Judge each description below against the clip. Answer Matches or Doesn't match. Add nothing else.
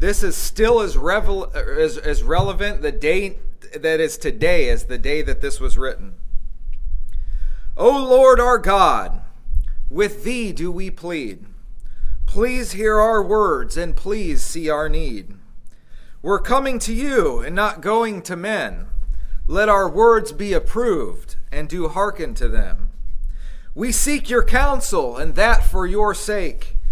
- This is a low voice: Doesn't match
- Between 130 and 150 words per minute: Matches